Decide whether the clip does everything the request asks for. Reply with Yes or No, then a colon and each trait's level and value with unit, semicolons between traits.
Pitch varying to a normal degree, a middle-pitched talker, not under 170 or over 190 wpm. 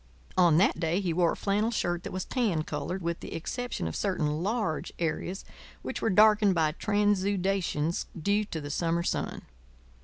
Yes: average, 3.8 semitones; medium, 180 Hz; average, 175 wpm